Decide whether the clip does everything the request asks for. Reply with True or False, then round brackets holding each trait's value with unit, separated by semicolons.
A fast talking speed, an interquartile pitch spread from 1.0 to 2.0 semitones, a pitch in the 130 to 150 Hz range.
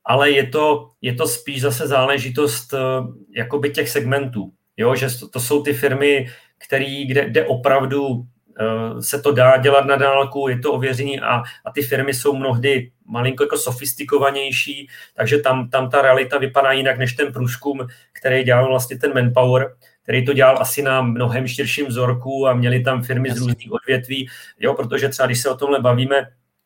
True (180 wpm; 1.7 semitones; 135 Hz)